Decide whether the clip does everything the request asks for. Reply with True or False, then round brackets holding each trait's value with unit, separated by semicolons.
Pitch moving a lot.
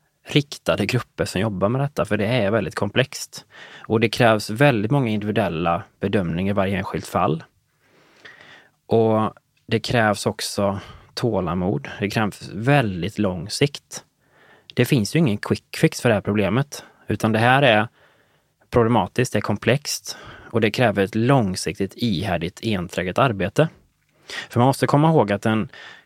False (3.5 semitones)